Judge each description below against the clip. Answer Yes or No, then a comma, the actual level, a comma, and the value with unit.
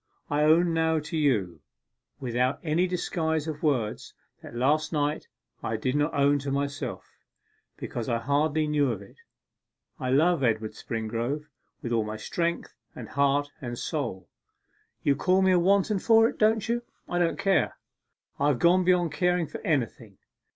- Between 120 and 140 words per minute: No, average, 165 wpm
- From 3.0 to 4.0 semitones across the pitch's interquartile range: No, wide, 5.4 semitones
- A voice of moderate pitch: Yes, medium, 145 Hz